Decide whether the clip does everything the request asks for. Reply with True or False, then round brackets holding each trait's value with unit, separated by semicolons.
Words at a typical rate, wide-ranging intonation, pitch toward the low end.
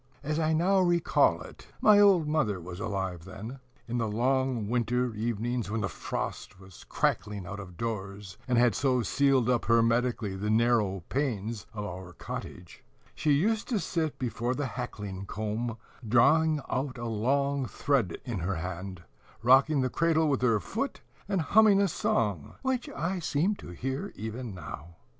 True (165 wpm; 5.9 semitones; 120 Hz)